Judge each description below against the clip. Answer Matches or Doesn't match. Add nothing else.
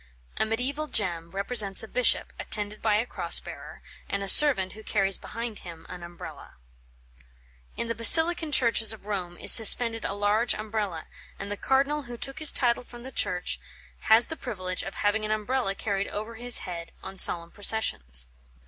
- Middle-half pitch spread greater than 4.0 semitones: Doesn't match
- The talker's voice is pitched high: Matches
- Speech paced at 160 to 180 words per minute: Matches